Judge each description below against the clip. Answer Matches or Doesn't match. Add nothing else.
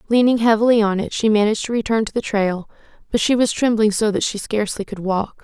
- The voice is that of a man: Doesn't match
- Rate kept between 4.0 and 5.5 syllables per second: Doesn't match